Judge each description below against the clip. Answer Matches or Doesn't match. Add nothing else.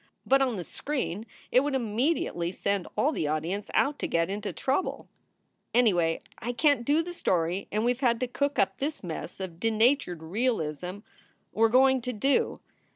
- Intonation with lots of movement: Matches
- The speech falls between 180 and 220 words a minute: Matches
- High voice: Matches